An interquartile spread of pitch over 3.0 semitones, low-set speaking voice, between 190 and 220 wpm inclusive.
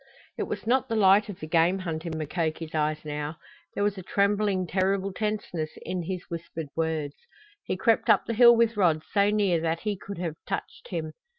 No: average, 4.1 semitones; medium, 185 Hz; average, 200 wpm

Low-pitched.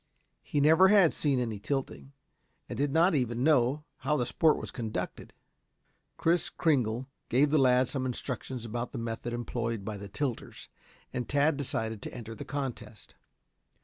Yes: low, 130 Hz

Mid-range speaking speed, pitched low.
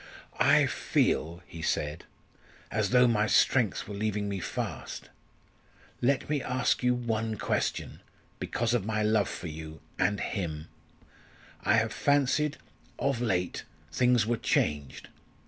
No: slow, 130 wpm; low, 110 Hz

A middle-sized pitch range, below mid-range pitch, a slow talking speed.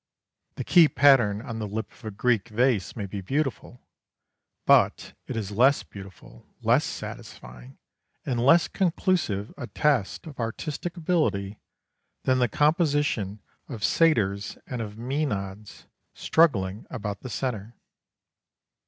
No: wide, 6.0 semitones; low, 115 Hz; slow, 125 wpm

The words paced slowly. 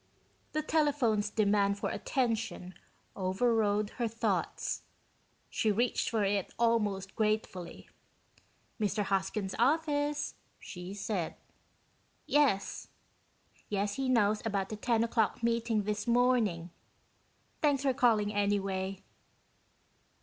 Yes: slow, 100 wpm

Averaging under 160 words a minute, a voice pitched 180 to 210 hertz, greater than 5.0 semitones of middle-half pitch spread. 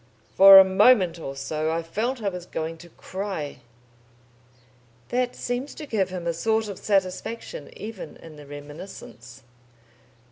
Yes: average, 145 wpm; medium, 185 Hz; wide, 5.4 semitones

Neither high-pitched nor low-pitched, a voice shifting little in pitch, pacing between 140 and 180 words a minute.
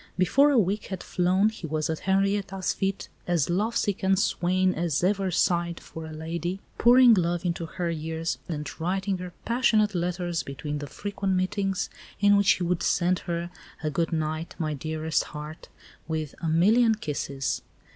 No: medium, 175 Hz; average, 3.4 semitones; average, 165 wpm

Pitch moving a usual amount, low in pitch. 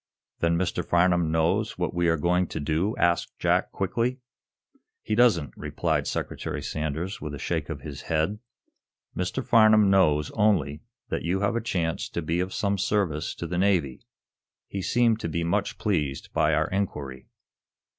Yes: average, 4.2 semitones; very low, 90 Hz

